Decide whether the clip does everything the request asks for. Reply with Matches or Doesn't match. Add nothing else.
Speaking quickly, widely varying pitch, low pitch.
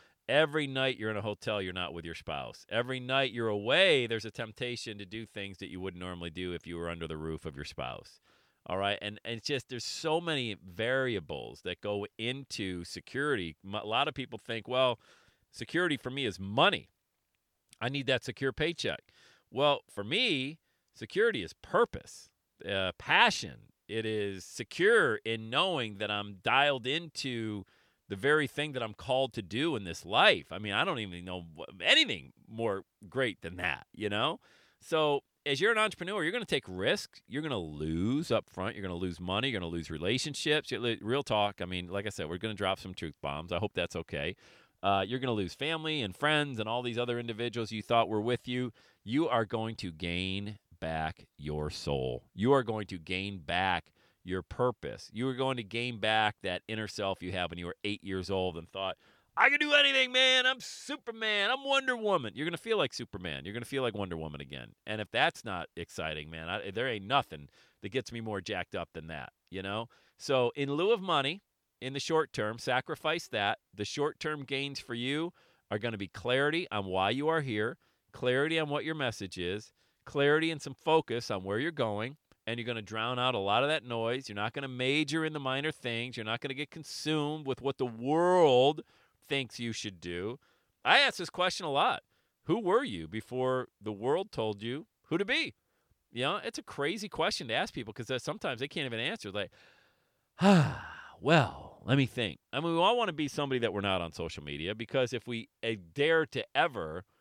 Matches